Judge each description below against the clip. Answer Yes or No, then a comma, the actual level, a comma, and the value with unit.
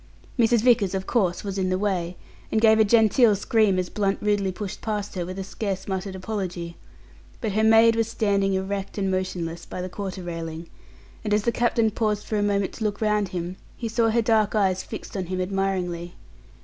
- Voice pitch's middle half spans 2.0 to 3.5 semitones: Yes, average, 2.8 semitones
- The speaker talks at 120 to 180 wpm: No, fast, 205 wpm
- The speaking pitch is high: Yes, high, 200 Hz